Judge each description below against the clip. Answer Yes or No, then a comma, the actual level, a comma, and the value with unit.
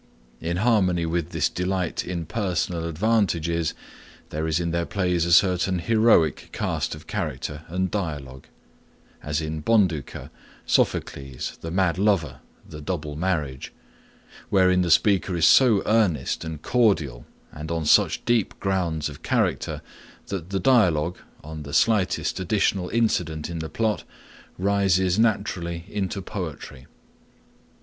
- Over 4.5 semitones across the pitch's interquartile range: No, average, 3.6 semitones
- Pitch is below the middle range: Yes, very low, 85 Hz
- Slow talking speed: Yes, slow, 125 wpm